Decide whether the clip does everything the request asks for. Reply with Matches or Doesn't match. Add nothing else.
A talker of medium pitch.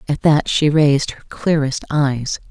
Matches